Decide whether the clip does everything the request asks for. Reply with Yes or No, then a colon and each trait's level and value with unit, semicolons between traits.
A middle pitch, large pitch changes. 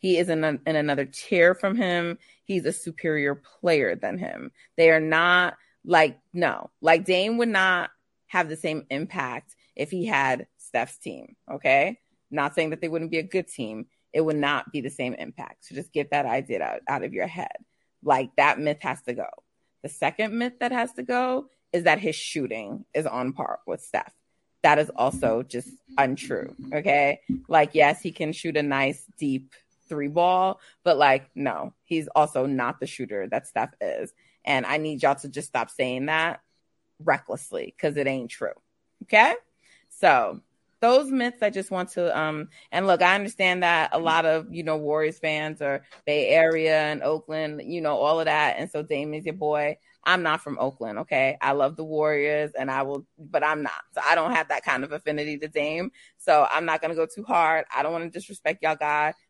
No: medium, 155 Hz; average, 3.2 semitones